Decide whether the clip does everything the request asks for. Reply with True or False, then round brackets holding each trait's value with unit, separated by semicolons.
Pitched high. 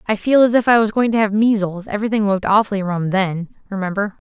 True (205 Hz)